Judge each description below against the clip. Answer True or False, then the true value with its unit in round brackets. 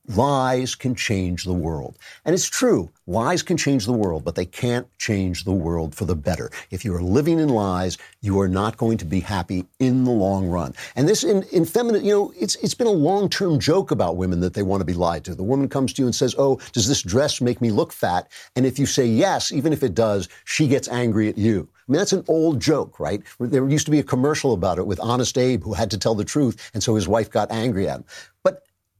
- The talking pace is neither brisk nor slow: False (255 wpm)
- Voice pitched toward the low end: True (120 Hz)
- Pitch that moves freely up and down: True (6.1 semitones)